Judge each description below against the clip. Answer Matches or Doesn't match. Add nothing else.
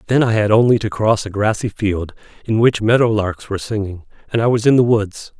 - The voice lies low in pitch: Matches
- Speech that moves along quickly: Matches